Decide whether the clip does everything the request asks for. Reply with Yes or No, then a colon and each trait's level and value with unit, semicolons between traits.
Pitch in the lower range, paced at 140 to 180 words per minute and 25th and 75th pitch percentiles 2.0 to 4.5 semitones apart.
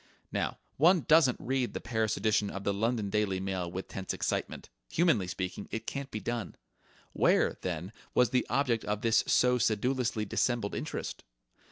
Yes: low, 110 Hz; average, 165 wpm; average, 3.9 semitones